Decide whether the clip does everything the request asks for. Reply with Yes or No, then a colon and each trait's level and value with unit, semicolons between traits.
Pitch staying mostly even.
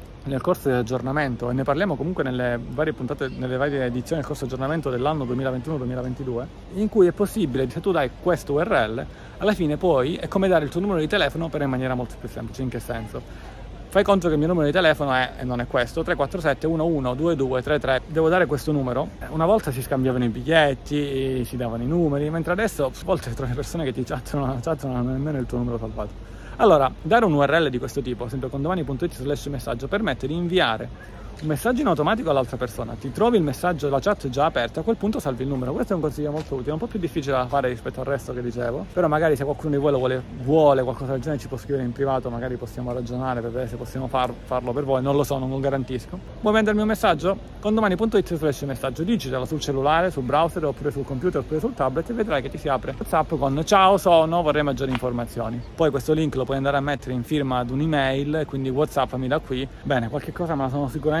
No: average, 4.1 semitones